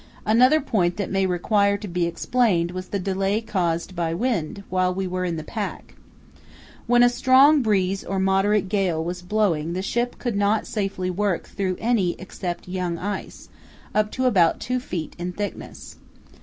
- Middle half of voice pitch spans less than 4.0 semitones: Yes, average, 3.2 semitones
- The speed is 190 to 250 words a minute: No, average, 170 wpm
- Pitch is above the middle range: Yes, high, 195 Hz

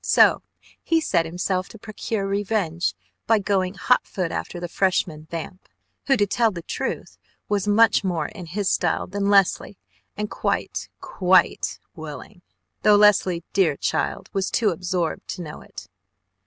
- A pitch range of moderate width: Yes, average, 3.0 semitones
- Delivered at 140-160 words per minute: Yes, average, 155 wpm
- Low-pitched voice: No, high, 190 Hz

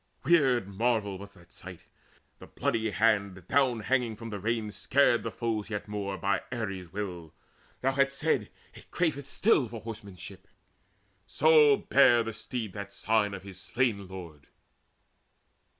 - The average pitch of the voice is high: No, low, 110 Hz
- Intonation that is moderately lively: Yes, average, 4.0 semitones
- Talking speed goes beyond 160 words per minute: No, average, 150 wpm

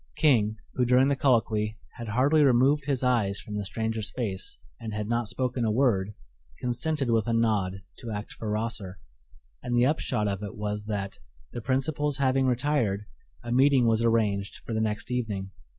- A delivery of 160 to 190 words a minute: Yes, average, 180 wpm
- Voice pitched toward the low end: Yes, low, 115 Hz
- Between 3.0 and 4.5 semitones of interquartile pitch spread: Yes, average, 3.5 semitones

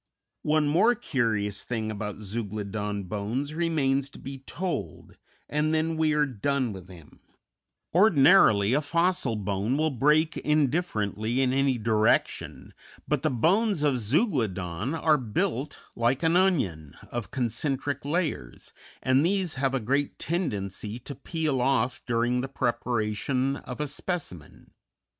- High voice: No, low, 135 Hz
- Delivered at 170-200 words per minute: No, slow, 135 wpm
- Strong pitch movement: Yes, wide, 5.9 semitones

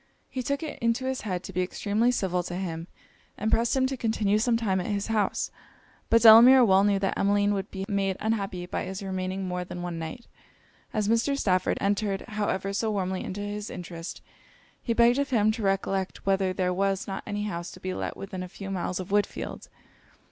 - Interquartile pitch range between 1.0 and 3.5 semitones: Yes, average, 2.9 semitones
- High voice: Yes, high, 200 Hz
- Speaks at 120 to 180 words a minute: No, fast, 205 wpm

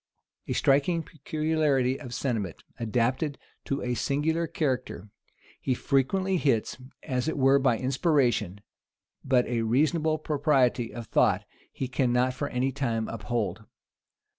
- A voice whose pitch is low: Yes, low, 130 Hz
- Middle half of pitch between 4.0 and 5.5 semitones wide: No, average, 3.4 semitones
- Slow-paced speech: Yes, slow, 125 wpm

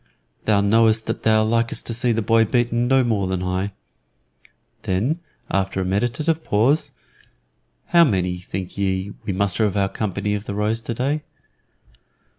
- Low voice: Yes, low, 110 Hz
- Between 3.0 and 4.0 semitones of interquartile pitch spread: Yes, average, 3.4 semitones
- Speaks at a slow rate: No, average, 155 wpm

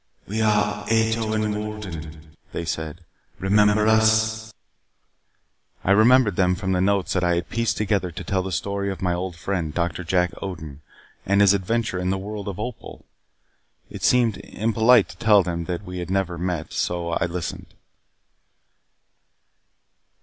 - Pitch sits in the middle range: No, very low, 95 Hz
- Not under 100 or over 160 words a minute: Yes, average, 155 wpm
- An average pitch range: Yes, average, 3.5 semitones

